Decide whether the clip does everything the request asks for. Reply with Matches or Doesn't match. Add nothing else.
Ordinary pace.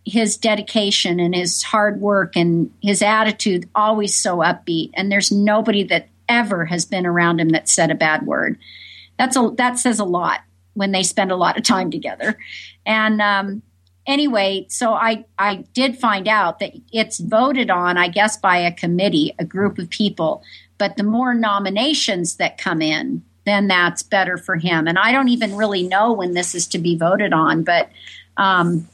Matches